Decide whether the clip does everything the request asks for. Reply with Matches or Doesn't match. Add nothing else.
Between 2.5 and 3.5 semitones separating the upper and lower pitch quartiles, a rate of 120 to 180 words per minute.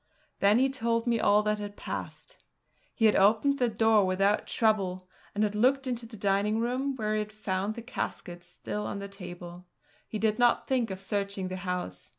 Doesn't match